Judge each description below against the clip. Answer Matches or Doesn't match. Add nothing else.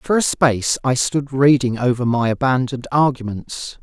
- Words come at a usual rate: Matches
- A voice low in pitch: Matches